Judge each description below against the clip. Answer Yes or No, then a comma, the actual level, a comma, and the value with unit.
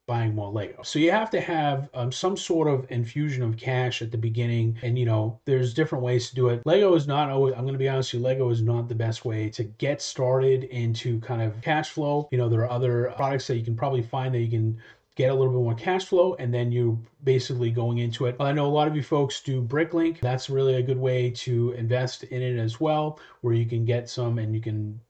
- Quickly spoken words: Yes, fast, 260 wpm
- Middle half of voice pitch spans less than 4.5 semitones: Yes, average, 2.9 semitones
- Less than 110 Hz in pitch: No, low, 125 Hz